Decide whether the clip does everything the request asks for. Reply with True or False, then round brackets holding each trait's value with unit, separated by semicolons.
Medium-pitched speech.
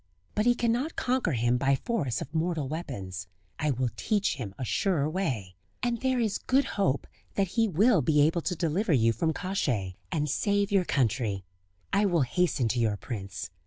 True (155 Hz)